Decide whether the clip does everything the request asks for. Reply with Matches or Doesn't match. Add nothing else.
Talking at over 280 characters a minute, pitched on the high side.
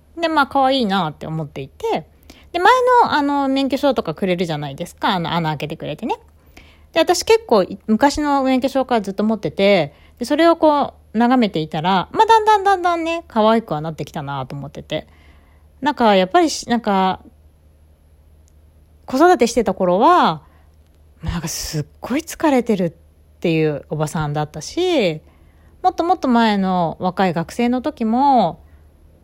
Matches